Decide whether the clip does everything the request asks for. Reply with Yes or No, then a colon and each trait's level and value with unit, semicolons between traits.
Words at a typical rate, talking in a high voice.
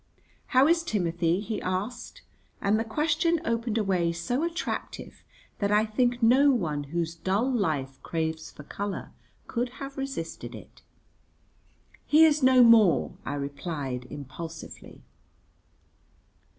No: slow, 125 wpm; high, 210 Hz